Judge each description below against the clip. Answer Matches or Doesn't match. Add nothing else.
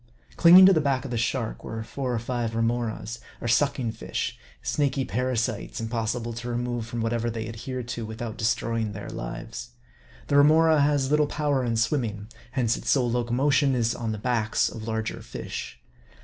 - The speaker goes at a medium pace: Matches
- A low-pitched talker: Matches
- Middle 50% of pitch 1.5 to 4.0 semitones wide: Matches